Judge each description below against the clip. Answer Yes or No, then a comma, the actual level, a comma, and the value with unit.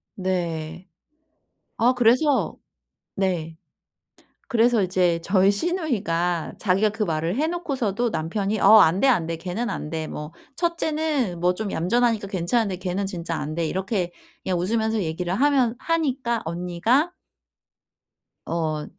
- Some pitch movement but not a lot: No, wide, 5.8 semitones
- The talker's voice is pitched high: Yes, high, 195 Hz